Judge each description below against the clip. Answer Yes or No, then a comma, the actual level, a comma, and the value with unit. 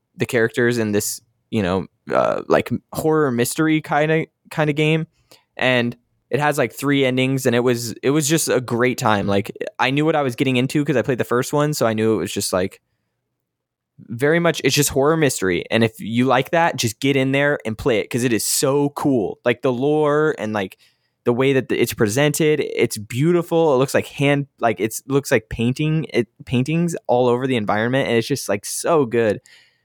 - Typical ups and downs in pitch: Yes, average, 3.9 semitones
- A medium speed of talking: No, fast, 215 wpm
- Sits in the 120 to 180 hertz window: Yes, low, 130 Hz